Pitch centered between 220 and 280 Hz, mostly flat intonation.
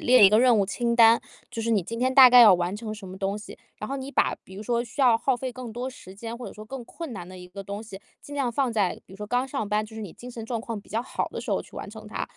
No: high, 225 Hz; average, 3.2 semitones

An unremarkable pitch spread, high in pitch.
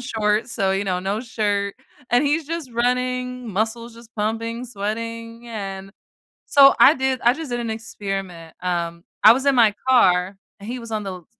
Yes: average, 3.8 semitones; high, 225 Hz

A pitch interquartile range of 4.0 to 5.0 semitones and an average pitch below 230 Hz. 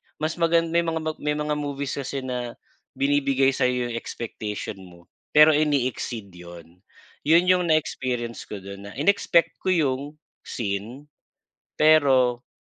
Yes: average, 4.7 semitones; low, 135 Hz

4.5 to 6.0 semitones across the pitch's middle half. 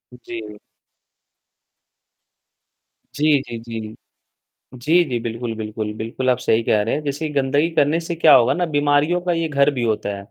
Yes: average, 4.8 semitones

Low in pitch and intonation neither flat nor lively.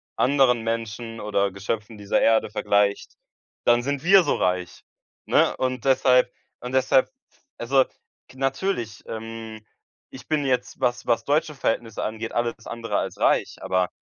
Yes: low, 115 Hz; average, 3.2 semitones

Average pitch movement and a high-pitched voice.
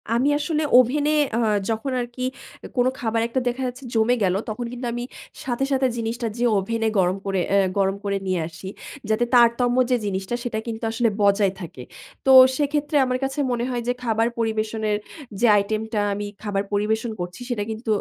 Yes: average, 3.1 semitones; high, 225 Hz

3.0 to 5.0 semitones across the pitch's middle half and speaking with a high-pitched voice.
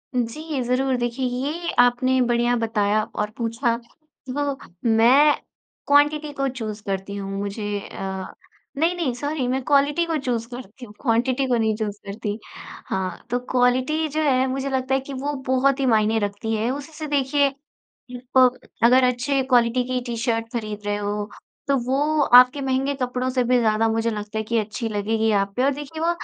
Yes: average, 3.6 semitones; very high, 250 Hz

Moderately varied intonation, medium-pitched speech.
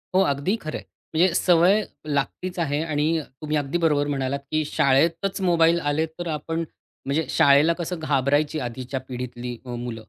Yes: average, 3.2 semitones; medium, 150 Hz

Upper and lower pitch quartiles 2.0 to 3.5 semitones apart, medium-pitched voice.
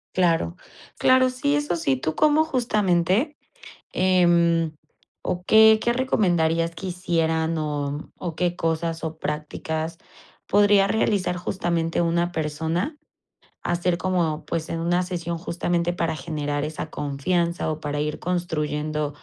Yes: narrow, 2.5 semitones; medium, 170 Hz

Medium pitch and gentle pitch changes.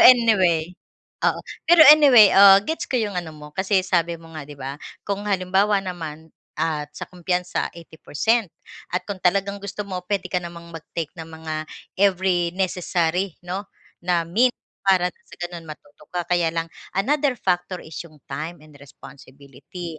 No: medium, 180 Hz; average, 3.4 semitones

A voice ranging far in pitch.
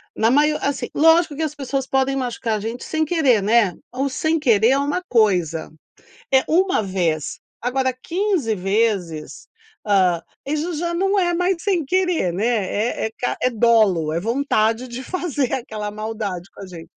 Yes: wide, 6.6 semitones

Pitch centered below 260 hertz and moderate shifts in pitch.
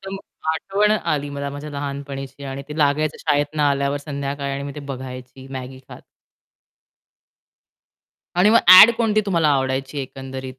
No: medium, 140 Hz; narrow, 2.1 semitones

